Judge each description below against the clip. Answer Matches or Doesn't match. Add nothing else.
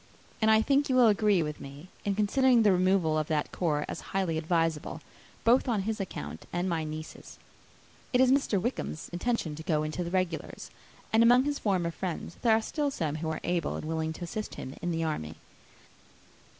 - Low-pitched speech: Doesn't match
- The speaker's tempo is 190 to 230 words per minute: Matches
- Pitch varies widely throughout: Matches